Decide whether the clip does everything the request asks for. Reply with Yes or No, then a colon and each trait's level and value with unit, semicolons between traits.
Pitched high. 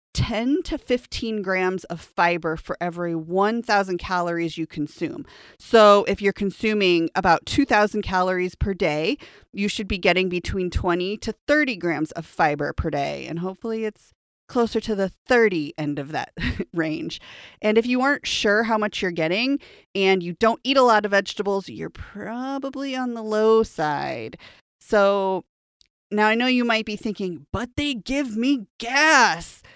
Yes: high, 205 Hz